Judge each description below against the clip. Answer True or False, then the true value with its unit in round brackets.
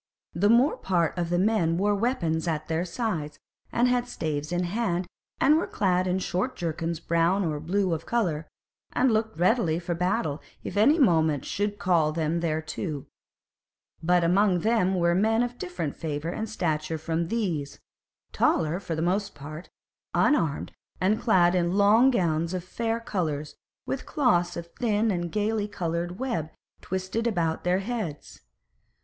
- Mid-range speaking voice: True (180 Hz)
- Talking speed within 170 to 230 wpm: False (160 wpm)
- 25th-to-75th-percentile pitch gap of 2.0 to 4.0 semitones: False (4.4 semitones)